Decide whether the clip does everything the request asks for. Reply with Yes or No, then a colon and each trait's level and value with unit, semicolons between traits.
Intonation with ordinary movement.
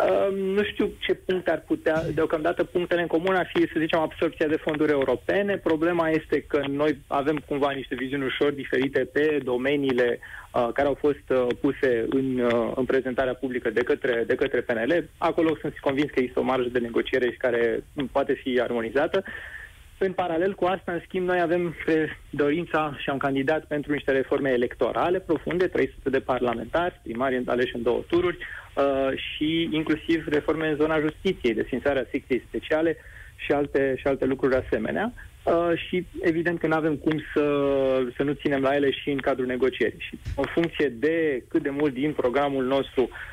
Yes: average, 3.5 semitones